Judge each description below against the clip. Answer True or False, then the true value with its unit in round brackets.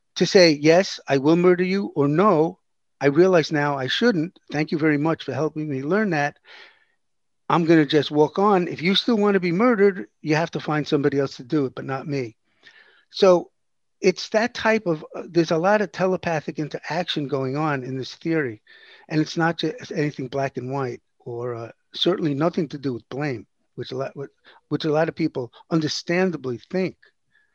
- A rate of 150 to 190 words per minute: False (200 wpm)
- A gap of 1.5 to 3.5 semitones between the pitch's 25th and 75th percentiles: False (4.2 semitones)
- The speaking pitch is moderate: True (160 Hz)